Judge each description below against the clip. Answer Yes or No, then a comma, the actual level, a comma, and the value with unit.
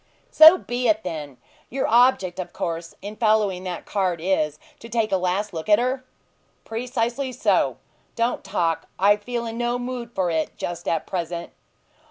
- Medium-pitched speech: No, high, 205 Hz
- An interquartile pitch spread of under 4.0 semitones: No, wide, 5.4 semitones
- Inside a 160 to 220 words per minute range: Yes, average, 170 wpm